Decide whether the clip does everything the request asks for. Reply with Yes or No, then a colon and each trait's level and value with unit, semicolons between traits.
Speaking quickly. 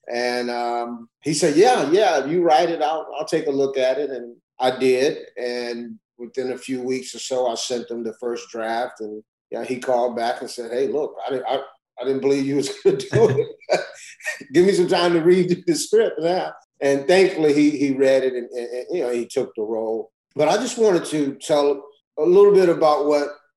Yes: fast, 230 wpm